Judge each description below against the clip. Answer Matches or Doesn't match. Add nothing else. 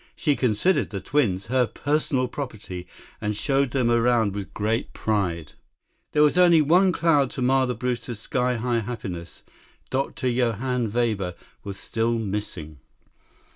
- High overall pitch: Doesn't match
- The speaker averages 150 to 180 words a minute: Doesn't match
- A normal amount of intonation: Matches